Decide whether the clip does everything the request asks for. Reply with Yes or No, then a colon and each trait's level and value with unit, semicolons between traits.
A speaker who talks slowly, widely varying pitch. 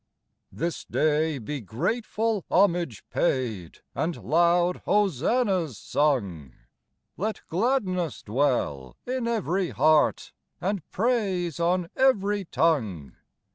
Yes: slow, 95 wpm; wide, 6.3 semitones